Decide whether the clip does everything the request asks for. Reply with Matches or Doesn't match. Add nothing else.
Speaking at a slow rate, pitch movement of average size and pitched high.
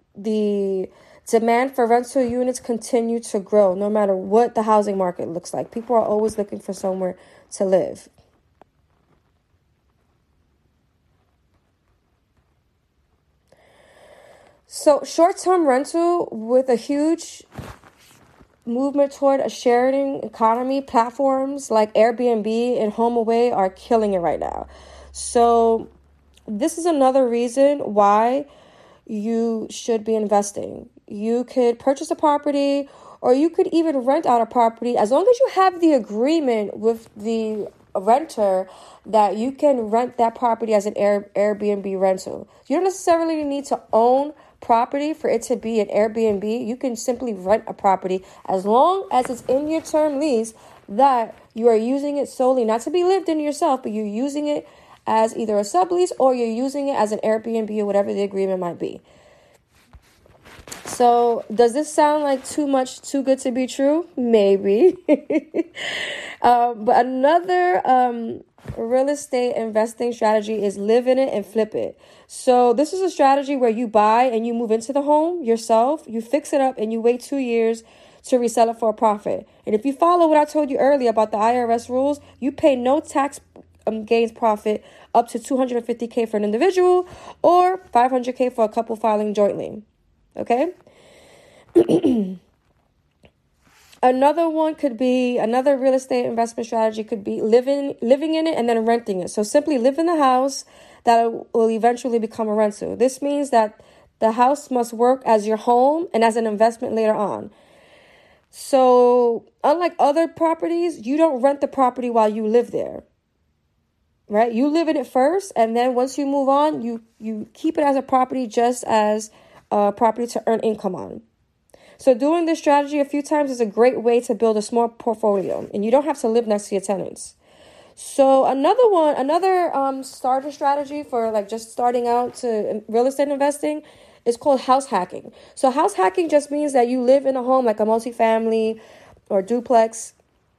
Doesn't match